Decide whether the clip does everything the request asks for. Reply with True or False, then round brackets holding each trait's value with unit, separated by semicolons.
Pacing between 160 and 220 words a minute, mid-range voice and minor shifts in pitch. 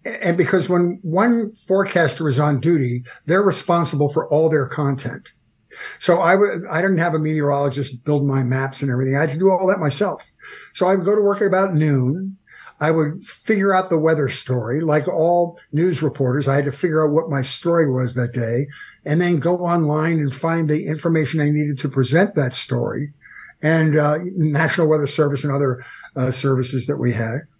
False (200 wpm; 155 Hz; 3.7 semitones)